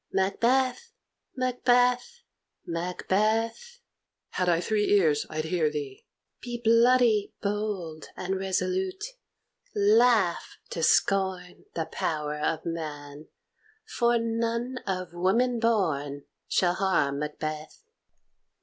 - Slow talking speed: Yes, slow, 95 wpm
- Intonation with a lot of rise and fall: Yes, wide, 6.4 semitones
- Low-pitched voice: No, high, 195 Hz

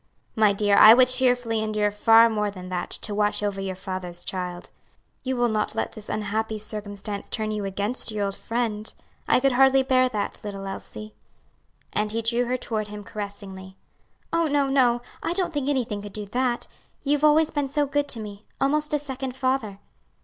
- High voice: Yes, high, 220 Hz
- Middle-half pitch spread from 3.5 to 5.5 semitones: Yes, average, 4.1 semitones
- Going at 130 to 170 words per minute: No, average, 190 wpm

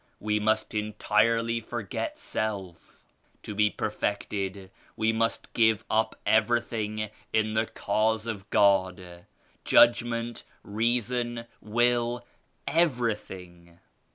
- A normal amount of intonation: No, narrow, 2.3 semitones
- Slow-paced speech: Yes, slow, 100 wpm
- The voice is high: No, low, 110 Hz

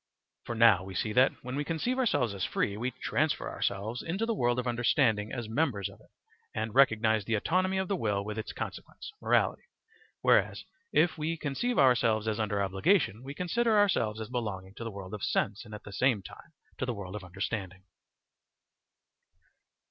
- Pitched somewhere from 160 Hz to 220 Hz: No, low, 115 Hz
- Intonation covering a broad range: Yes, wide, 5.8 semitones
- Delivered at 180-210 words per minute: Yes, average, 185 wpm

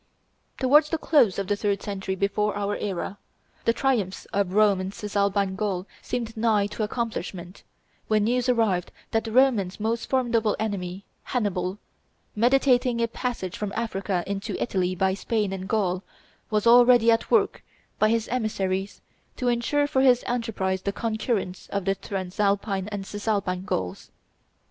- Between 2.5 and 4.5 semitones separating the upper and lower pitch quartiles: Yes, average, 3.3 semitones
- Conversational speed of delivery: Yes, average, 150 wpm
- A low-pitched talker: No, high, 210 Hz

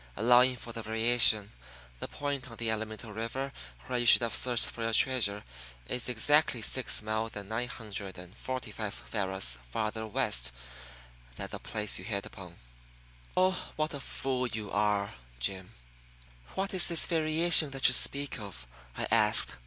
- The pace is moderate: Yes, average, 165 wpm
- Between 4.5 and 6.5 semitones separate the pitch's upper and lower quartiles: No, average, 3.7 semitones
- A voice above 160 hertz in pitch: No, low, 115 Hz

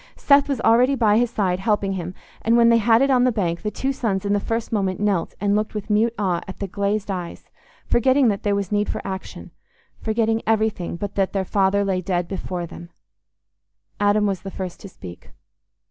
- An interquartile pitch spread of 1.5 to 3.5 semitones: Yes, average, 2.9 semitones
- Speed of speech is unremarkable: No, fast, 210 wpm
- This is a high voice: Yes, high, 205 Hz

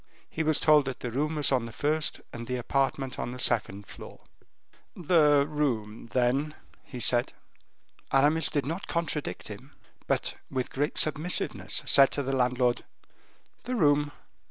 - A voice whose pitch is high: No, medium, 140 Hz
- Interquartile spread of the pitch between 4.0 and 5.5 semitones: No, average, 3.4 semitones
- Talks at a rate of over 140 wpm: Yes, average, 155 wpm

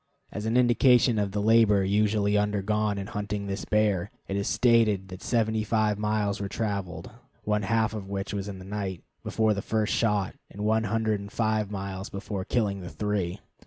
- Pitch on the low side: Yes, low, 105 Hz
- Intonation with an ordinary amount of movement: No, narrow, 1.7 semitones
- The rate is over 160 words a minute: Yes, average, 190 wpm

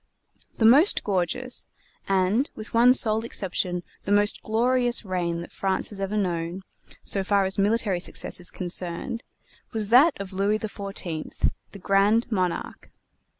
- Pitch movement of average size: Yes, average, 3.4 semitones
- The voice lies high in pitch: Yes, high, 200 Hz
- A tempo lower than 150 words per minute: Yes, average, 140 wpm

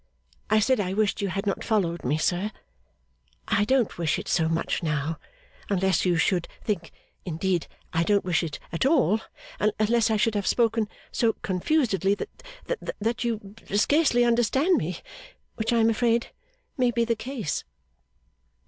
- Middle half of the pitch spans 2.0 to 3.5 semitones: No, average, 4.6 semitones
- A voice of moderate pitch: No, high, 210 Hz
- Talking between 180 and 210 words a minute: No, average, 160 wpm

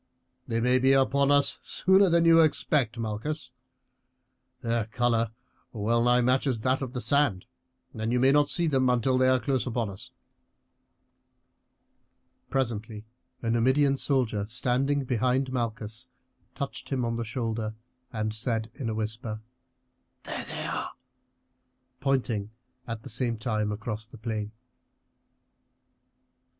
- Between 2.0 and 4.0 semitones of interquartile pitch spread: Yes, average, 3.2 semitones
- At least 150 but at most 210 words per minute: No, slow, 135 wpm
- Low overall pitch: Yes, low, 120 Hz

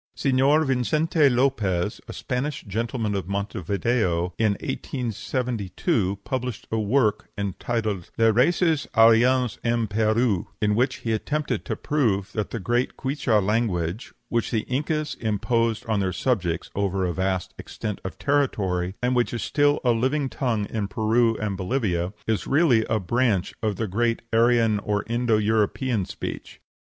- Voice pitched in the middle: No, low, 115 Hz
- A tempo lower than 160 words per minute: Yes, average, 145 wpm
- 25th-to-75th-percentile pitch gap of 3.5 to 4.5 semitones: Yes, average, 3.9 semitones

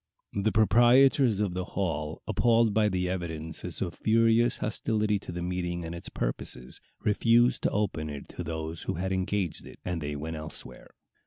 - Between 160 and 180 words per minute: Yes, average, 170 wpm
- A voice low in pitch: Yes, very low, 95 Hz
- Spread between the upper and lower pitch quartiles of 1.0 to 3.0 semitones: No, average, 4.9 semitones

